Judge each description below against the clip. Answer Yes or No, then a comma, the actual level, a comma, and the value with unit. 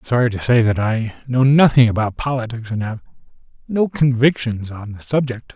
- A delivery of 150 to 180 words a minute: No, average, 195 wpm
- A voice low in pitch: Yes, low, 120 Hz